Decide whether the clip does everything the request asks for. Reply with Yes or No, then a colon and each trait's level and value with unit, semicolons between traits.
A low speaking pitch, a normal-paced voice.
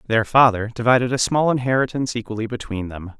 Yes: low, 115 Hz; average, 170 wpm